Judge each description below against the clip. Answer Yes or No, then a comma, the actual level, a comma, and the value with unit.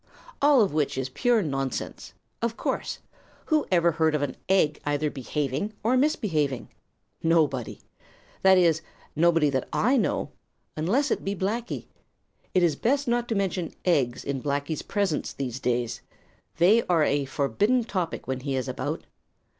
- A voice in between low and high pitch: Yes, medium, 165 Hz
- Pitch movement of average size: No, wide, 6.7 semitones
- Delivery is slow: No, average, 155 wpm